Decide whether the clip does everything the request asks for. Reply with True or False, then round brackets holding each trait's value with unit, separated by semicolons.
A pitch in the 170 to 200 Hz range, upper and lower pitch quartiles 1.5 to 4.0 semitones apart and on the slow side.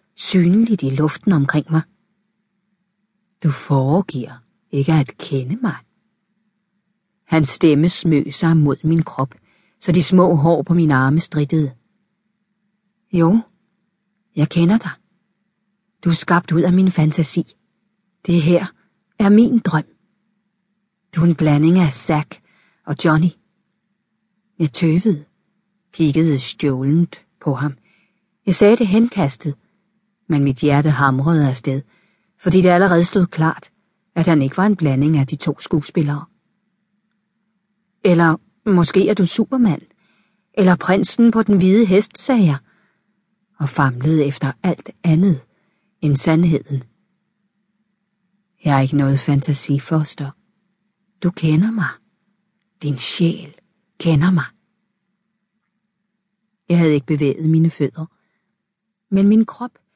False (190 Hz; 4.7 semitones; 120 wpm)